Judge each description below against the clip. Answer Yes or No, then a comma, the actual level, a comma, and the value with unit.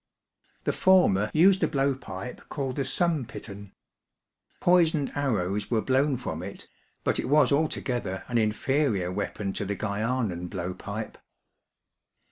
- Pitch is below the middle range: Yes, low, 120 Hz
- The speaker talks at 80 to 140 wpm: Yes, slow, 135 wpm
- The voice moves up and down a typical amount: No, wide, 6.2 semitones